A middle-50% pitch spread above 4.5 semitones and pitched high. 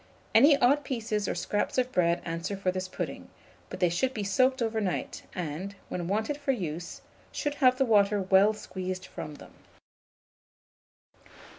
Yes: wide, 5.6 semitones; high, 205 Hz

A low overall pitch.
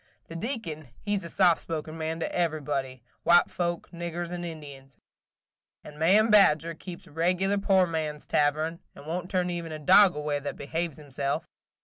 No: medium, 165 Hz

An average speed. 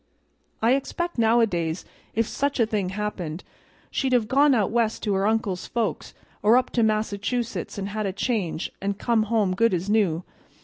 Yes: average, 175 wpm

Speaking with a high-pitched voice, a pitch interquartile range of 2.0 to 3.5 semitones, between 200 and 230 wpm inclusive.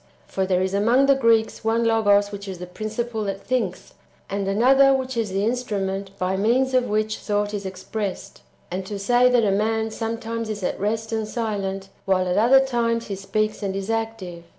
Yes: high, 215 Hz; average, 2.8 semitones; fast, 205 wpm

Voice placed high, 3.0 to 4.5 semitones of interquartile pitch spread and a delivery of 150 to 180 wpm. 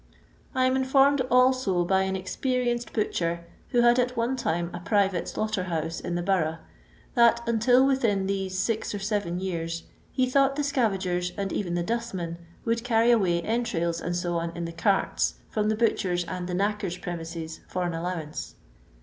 No: high, 195 Hz; average, 5.3 semitones; average, 175 wpm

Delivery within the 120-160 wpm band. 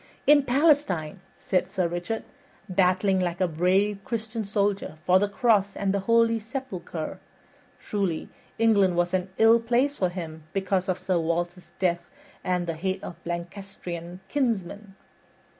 Yes: average, 145 wpm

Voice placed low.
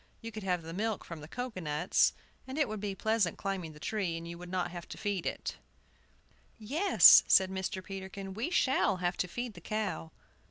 No: high, 190 Hz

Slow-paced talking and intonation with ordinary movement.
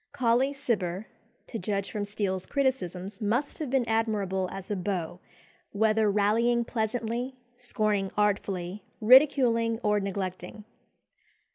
Yes: slow, 115 wpm; average, 3.4 semitones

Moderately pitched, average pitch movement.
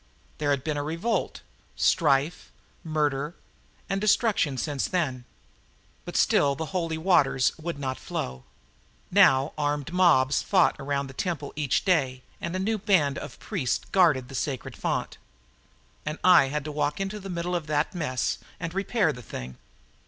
Yes: medium, 150 Hz; average, 4.6 semitones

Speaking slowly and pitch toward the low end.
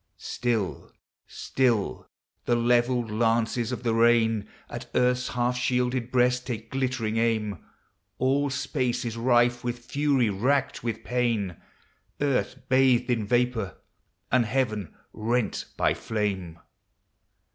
Yes: slow, 115 wpm; low, 120 Hz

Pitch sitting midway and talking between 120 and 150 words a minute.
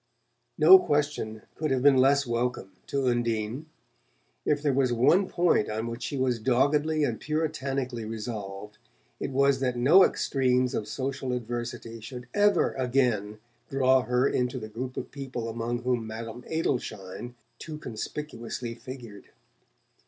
No: low, 125 Hz; average, 140 wpm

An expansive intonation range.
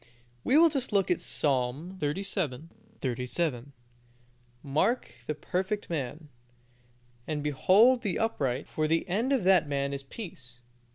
Yes: wide, 6.2 semitones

